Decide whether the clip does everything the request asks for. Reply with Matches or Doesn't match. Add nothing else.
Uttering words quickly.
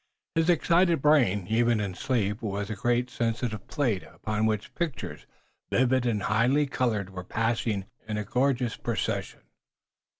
Doesn't match